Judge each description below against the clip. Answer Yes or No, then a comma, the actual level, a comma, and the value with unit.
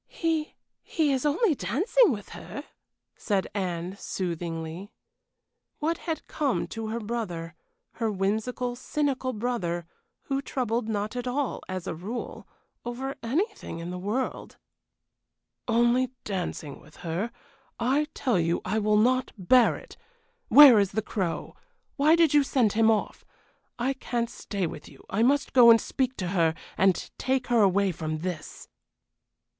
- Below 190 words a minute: Yes, average, 150 wpm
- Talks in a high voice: Yes, high, 225 Hz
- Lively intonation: Yes, wide, 5.8 semitones